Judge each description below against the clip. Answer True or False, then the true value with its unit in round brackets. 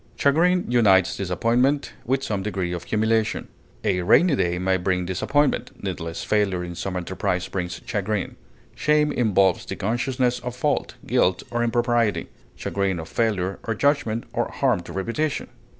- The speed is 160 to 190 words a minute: False (150 wpm)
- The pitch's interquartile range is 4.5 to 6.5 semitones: True (5.0 semitones)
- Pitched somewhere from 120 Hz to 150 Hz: False (105 Hz)